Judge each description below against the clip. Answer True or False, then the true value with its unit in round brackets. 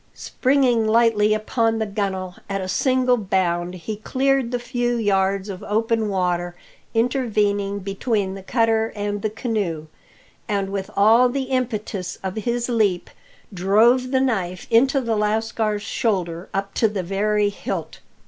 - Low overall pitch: False (215 Hz)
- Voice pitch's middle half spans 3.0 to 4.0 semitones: True (3.3 semitones)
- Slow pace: False (145 wpm)